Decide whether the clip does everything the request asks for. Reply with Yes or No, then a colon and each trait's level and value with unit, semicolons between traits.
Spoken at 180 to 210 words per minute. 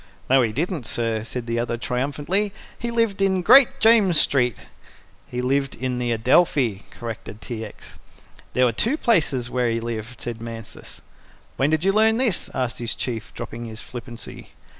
No: average, 170 wpm